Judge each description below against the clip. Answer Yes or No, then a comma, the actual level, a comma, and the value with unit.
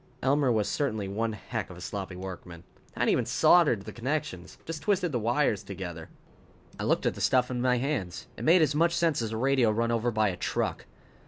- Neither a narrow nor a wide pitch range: No, wide, 6.3 semitones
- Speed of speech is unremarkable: No, fast, 215 wpm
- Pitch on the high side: No, low, 115 Hz